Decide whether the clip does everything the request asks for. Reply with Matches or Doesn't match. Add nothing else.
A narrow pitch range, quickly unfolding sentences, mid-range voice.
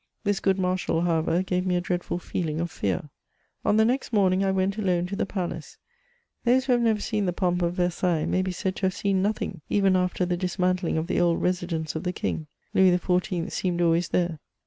Matches